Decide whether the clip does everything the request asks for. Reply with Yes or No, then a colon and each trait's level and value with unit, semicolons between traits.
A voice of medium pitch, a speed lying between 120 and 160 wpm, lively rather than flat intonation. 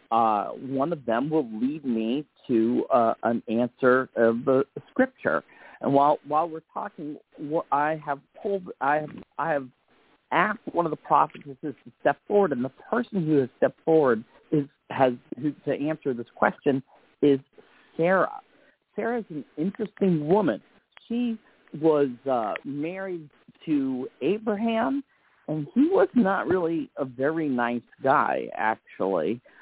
Yes: medium, 150 Hz; average, 145 wpm; wide, 6.3 semitones